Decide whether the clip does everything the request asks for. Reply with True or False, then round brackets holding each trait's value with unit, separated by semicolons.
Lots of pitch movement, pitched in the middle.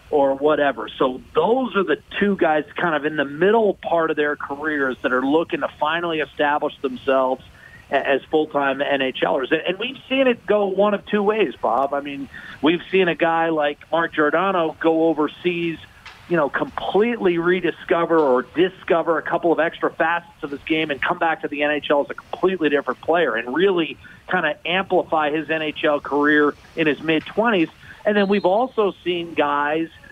False (3.2 semitones; 160 Hz)